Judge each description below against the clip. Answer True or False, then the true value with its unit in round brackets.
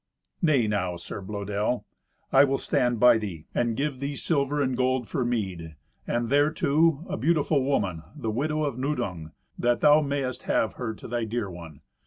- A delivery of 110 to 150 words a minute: False (175 wpm)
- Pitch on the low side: True (120 Hz)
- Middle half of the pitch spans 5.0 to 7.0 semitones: True (5.3 semitones)